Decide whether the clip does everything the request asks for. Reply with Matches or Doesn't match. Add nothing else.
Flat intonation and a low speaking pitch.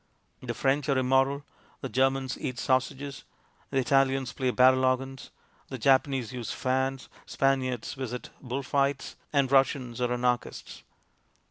Matches